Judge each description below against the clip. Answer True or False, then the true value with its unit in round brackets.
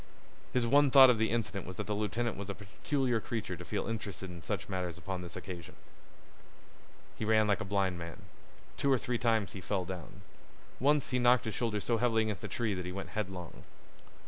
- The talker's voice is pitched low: True (105 Hz)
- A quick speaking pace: True (210 wpm)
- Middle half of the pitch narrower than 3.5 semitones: False (3.9 semitones)